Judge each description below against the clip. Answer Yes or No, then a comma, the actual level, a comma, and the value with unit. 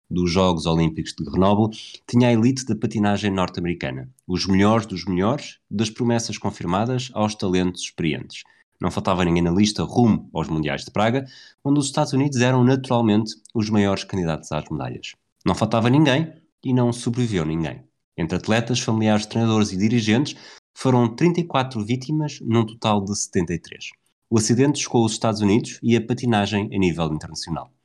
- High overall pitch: No, low, 110 Hz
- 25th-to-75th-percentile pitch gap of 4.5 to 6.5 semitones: Yes, average, 4.8 semitones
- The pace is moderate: Yes, average, 160 wpm